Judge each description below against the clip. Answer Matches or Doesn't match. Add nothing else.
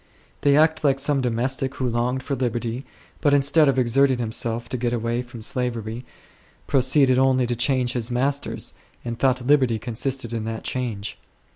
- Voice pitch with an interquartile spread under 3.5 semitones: Matches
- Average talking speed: Matches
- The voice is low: Matches